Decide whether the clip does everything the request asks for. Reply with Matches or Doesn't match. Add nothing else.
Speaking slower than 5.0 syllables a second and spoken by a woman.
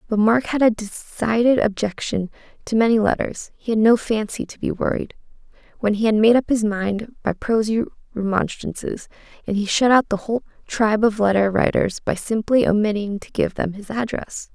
Doesn't match